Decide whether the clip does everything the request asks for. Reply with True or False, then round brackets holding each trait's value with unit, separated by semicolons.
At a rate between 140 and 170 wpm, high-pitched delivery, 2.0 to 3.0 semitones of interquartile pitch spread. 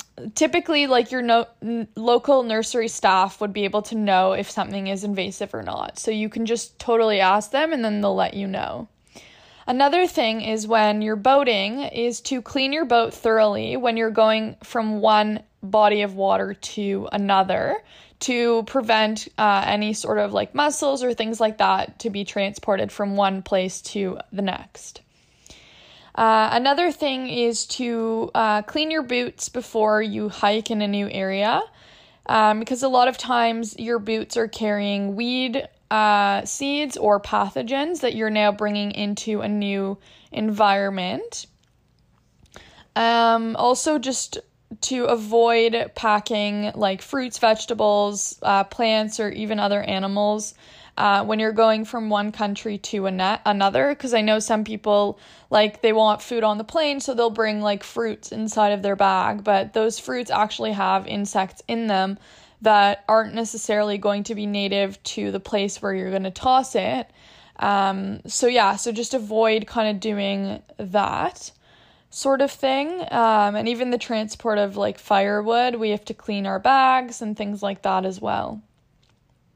True (165 wpm; 215 Hz; 2.5 semitones)